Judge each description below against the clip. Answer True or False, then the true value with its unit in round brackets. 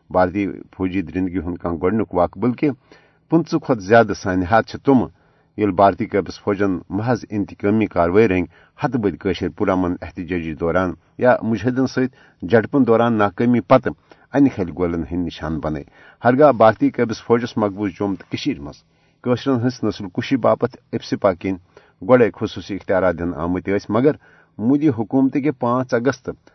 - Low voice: True (105 Hz)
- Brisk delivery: False (140 wpm)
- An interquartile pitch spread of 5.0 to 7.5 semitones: True (5.4 semitones)